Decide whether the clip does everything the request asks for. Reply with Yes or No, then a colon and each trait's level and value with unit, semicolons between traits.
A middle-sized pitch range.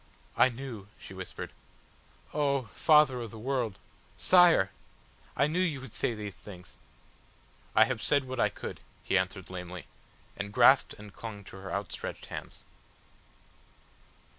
No: wide, 5.9 semitones